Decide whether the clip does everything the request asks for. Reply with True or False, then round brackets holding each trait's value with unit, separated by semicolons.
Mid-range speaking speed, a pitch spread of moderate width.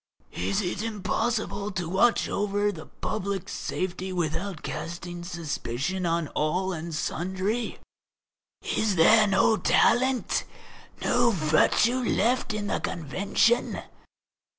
False (105 wpm; 3.9 semitones)